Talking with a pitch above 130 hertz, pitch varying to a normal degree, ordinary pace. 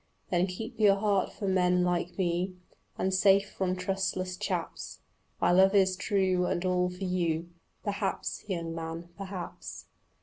No: medium, 185 Hz; narrow, 1.4 semitones; average, 145 wpm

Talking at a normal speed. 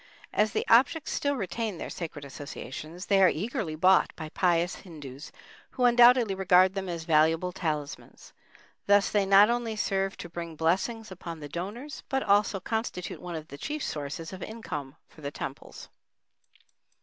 Yes: average, 160 wpm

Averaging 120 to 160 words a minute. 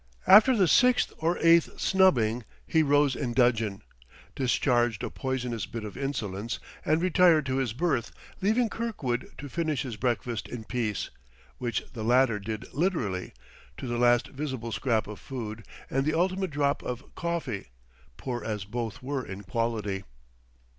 Yes: average, 155 wpm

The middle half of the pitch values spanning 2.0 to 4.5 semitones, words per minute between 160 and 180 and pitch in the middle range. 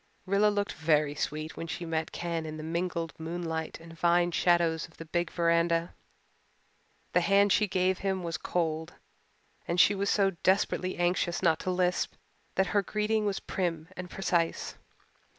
Yes: narrow, 2.4 semitones; average, 165 wpm; medium, 175 Hz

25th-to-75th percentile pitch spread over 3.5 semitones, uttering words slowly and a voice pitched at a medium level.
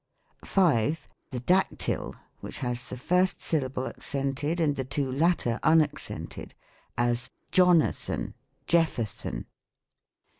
Yes: average, 5.0 semitones; slow, 105 wpm; medium, 145 Hz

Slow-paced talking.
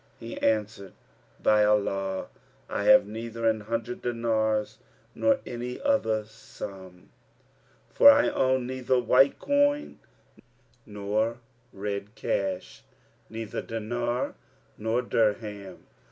Yes: slow, 100 wpm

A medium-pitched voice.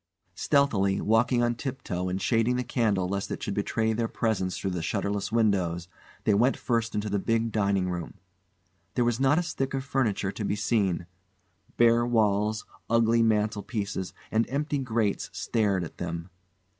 No: low, 110 Hz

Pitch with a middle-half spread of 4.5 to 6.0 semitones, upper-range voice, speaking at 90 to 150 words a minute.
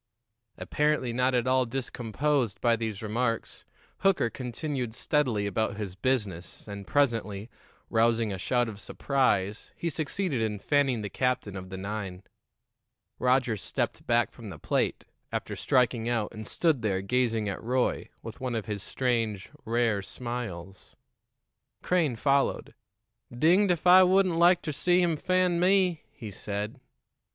No: average, 5.1 semitones; low, 120 Hz; average, 145 wpm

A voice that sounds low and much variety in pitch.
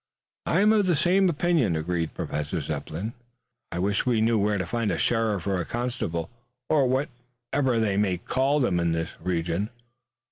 Yes: low, 110 Hz; wide, 6.9 semitones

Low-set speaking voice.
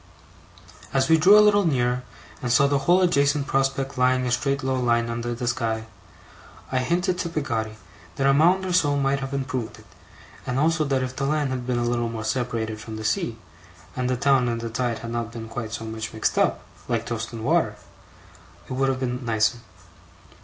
Yes: low, 125 Hz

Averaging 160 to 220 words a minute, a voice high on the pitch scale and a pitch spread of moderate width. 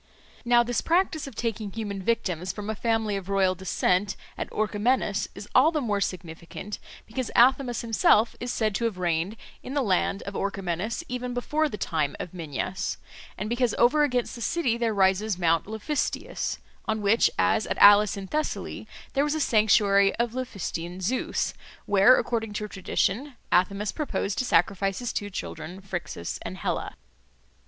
Yes: average, 165 wpm; high, 210 Hz; average, 4.0 semitones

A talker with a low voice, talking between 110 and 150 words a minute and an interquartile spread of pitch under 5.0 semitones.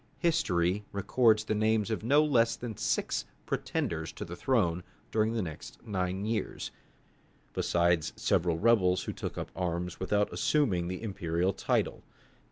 Yes: low, 100 Hz; average, 145 wpm; average, 4.3 semitones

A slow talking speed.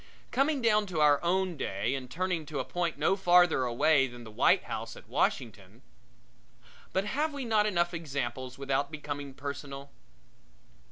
No: average, 160 wpm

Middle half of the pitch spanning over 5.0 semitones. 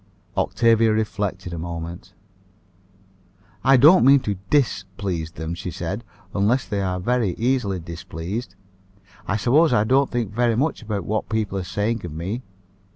No: average, 4.6 semitones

